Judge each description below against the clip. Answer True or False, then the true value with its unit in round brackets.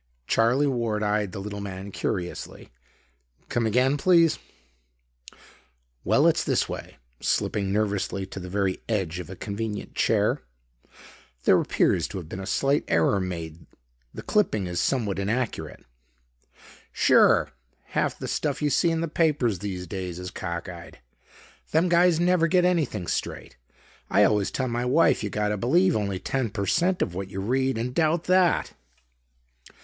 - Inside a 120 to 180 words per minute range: True (155 wpm)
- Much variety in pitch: True (6.8 semitones)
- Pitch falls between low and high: False (105 Hz)